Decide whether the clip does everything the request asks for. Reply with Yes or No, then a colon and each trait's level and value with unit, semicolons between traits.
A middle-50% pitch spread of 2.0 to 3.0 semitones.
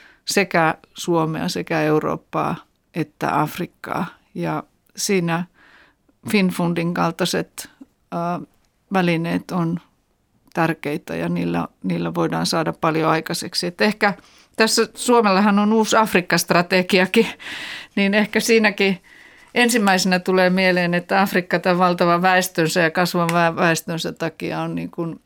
No: average, 3.4 semitones